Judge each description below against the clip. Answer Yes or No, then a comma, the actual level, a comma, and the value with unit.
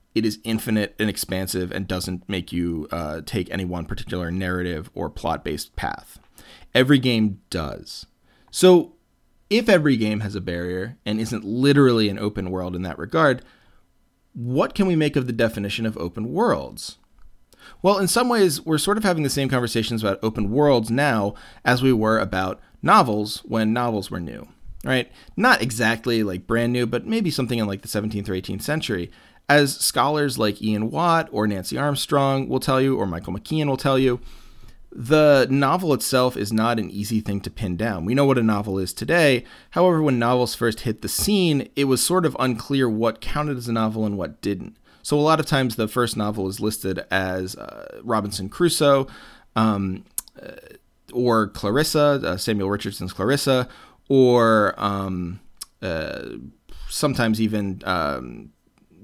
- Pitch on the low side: Yes, low, 115 Hz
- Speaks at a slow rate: No, average, 175 wpm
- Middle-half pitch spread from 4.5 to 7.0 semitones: Yes, average, 5.2 semitones